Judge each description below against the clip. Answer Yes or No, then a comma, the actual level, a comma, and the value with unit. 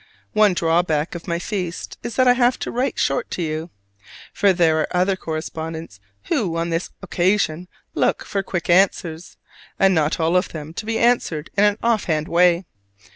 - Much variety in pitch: No, average, 3.6 semitones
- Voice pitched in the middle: Yes, medium, 175 Hz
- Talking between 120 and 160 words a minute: No, average, 180 wpm